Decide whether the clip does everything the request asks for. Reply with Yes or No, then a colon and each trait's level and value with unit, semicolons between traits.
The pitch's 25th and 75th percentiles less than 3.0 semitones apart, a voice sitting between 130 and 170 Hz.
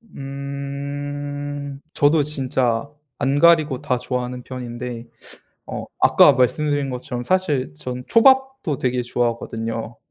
Yes: narrow, 2.6 semitones; low, 135 Hz